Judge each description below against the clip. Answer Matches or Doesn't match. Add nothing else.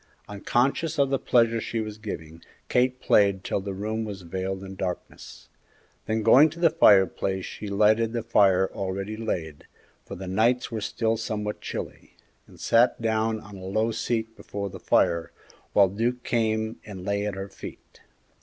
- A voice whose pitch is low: Matches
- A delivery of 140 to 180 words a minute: Matches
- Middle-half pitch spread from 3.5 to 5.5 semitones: Doesn't match